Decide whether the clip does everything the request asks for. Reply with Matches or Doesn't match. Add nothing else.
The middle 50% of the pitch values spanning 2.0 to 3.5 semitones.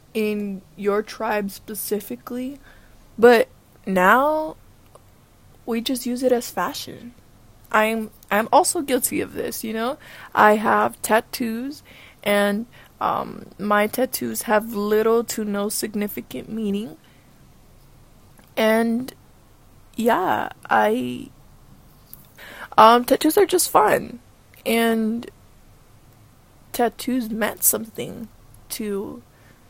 Matches